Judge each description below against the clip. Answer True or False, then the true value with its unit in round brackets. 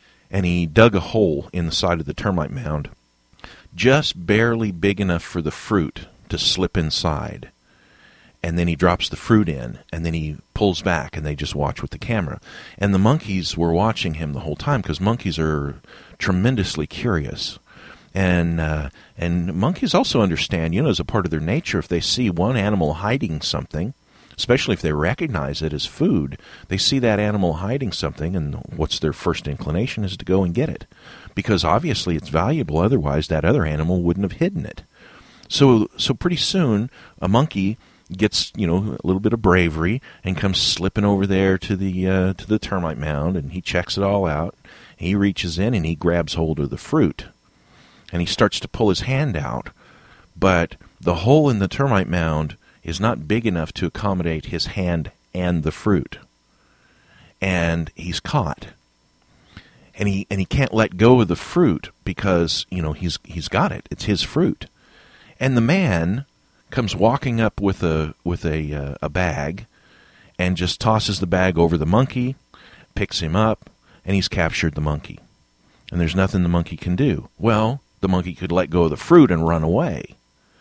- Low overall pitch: True (90 Hz)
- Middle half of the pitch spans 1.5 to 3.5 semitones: False (3.9 semitones)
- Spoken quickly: False (185 wpm)